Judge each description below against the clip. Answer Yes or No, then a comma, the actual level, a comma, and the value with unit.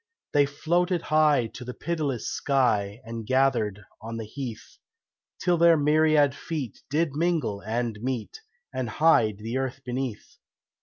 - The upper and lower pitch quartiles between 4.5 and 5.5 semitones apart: Yes, average, 5.2 semitones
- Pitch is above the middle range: No, low, 130 Hz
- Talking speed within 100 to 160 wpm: Yes, average, 140 wpm